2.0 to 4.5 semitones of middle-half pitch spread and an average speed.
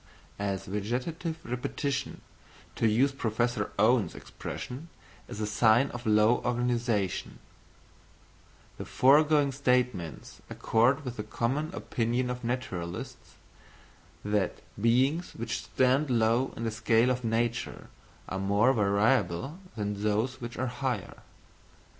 No: average, 3.3 semitones; slow, 115 wpm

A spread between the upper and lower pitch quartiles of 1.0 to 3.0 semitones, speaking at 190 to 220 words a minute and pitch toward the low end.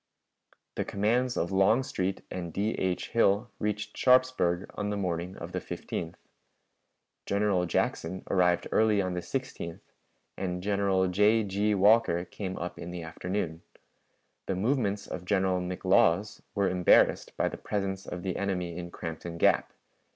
No: average, 2.7 semitones; average, 145 wpm; very low, 95 Hz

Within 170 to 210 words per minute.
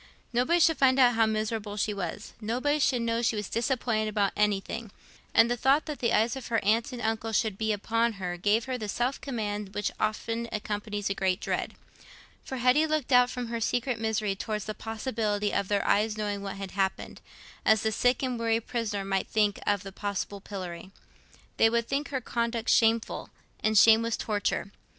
Yes: average, 195 wpm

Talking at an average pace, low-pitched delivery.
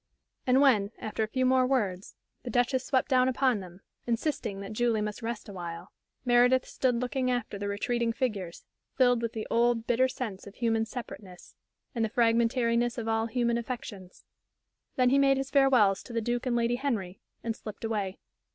No: average, 180 wpm; high, 235 Hz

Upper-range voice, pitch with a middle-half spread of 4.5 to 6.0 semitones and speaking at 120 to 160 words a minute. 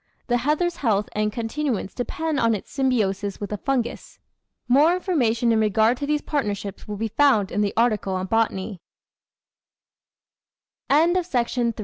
Yes: high, 225 Hz; average, 4.9 semitones; slow, 135 wpm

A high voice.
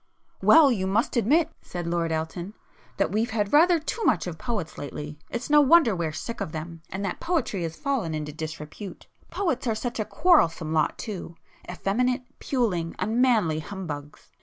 Yes: high, 200 Hz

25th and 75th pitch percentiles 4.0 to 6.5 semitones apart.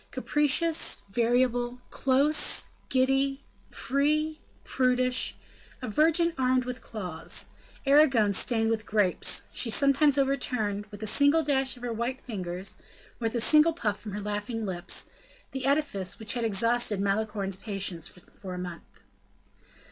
Yes: average, 4.8 semitones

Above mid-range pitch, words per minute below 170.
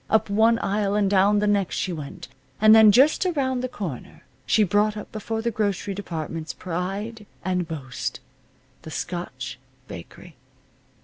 Yes: high, 205 Hz; average, 150 wpm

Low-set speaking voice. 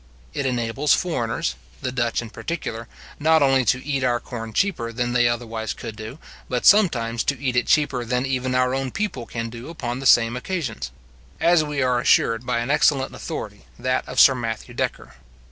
Yes: low, 125 Hz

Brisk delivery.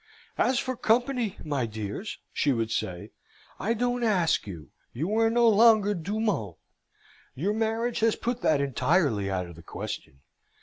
No: average, 160 wpm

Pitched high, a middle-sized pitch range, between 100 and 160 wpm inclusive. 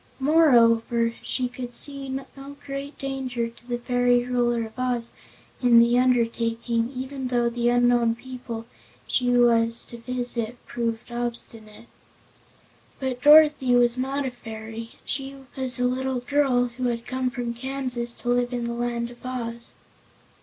No: high, 245 Hz; narrow, 1.5 semitones; average, 145 wpm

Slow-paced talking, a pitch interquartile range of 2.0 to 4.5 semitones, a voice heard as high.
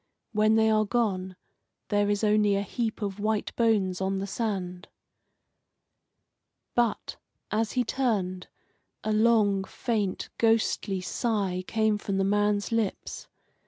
Yes: slow, 125 wpm; narrow, 2.4 semitones; high, 210 Hz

